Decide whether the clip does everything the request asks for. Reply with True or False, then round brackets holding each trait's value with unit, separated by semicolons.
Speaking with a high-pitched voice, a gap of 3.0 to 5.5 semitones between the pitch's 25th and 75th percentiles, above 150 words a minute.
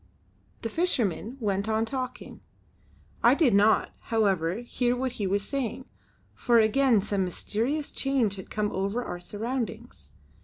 False (225 Hz; 4.1 semitones; 140 wpm)